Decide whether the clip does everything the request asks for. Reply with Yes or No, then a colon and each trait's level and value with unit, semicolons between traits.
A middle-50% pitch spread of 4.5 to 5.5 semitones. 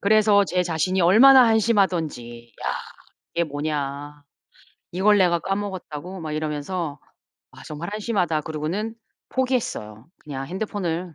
Yes: average, 5.2 semitones